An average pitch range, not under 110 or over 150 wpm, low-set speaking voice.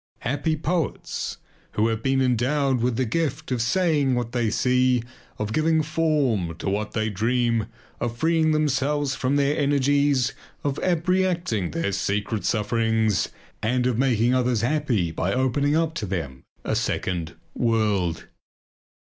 Yes: average, 4.9 semitones; average, 140 wpm; low, 125 Hz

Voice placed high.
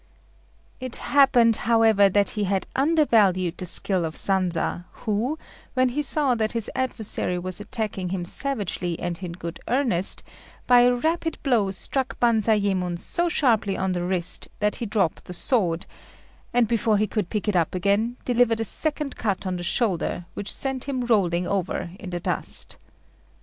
Yes: high, 210 Hz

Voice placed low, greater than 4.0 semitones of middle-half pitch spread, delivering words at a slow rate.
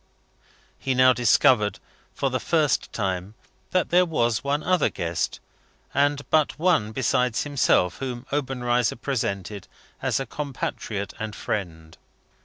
Yes: low, 125 Hz; average, 5.2 semitones; slow, 125 wpm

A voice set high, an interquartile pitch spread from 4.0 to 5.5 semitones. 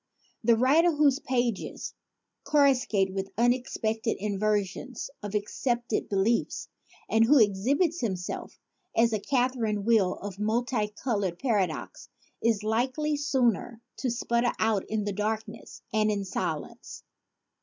No: high, 225 Hz; average, 3.5 semitones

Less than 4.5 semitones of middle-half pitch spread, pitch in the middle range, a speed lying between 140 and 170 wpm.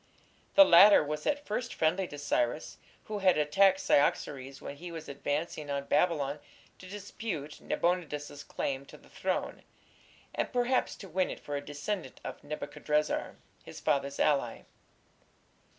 No: average, 4.9 semitones; medium, 150 Hz; average, 145 wpm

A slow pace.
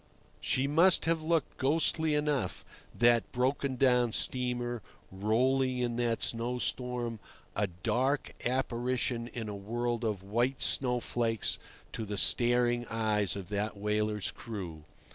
Yes: slow, 120 wpm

